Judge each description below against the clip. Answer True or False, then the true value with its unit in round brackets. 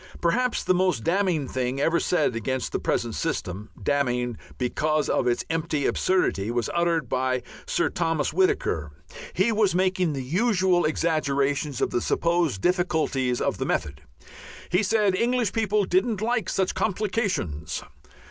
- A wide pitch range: True (6.4 semitones)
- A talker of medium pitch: True (170 Hz)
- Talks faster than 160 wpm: False (145 wpm)